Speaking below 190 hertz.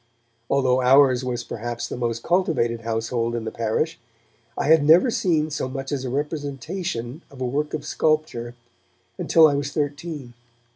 Yes: low, 135 Hz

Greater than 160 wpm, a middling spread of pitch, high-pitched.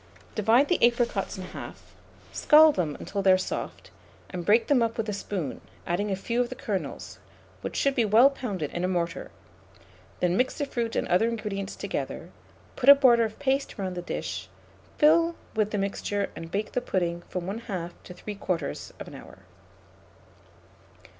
Yes: average, 175 wpm; average, 4.7 semitones; high, 210 Hz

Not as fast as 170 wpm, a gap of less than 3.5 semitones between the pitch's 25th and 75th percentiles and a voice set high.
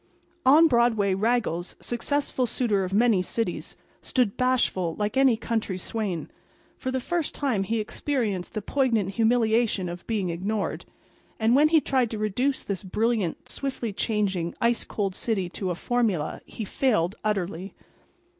No: average, 145 wpm; average, 4.2 semitones; high, 220 Hz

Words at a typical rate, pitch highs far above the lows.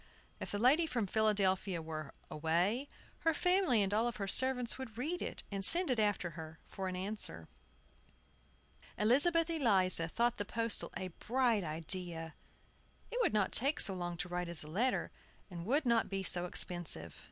Yes: average, 165 wpm; wide, 6.0 semitones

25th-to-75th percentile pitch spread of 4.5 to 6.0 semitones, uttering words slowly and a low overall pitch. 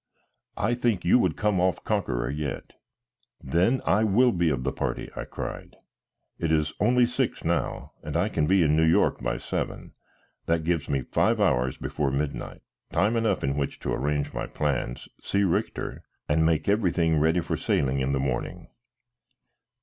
No: wide, 5.4 semitones; average, 175 wpm; very low, 80 Hz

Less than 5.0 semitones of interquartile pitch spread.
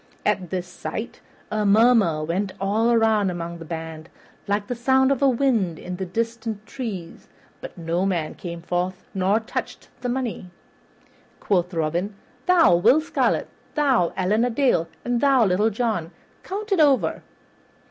No: wide, 5.5 semitones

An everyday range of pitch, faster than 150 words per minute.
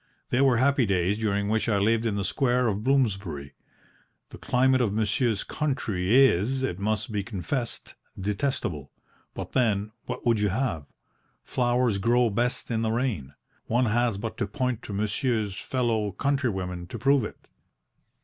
Yes: average, 4.1 semitones; average, 160 wpm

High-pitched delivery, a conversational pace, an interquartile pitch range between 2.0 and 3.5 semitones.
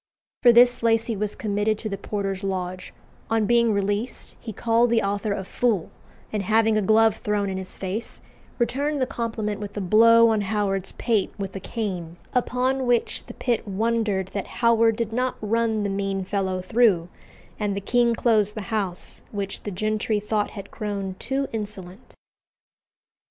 Yes: high, 215 Hz; average, 170 wpm; average, 2.7 semitones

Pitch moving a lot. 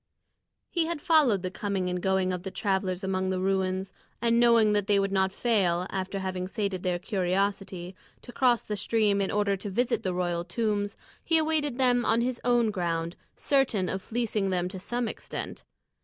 No: average, 3.9 semitones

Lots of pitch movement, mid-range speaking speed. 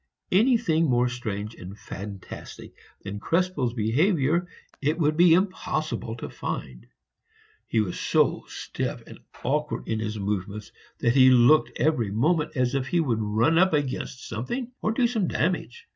Yes: wide, 7.1 semitones; average, 150 wpm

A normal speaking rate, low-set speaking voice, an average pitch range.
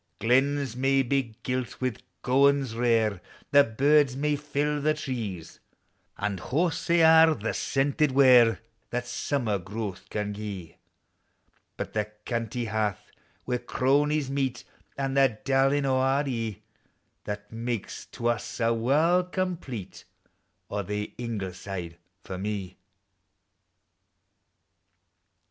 No: slow, 120 wpm; low, 125 Hz; average, 4.6 semitones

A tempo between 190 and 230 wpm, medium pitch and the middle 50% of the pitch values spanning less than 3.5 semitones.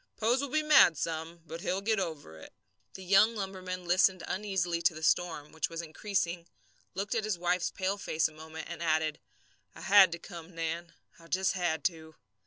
Yes: average, 195 wpm; medium, 175 Hz; average, 3.0 semitones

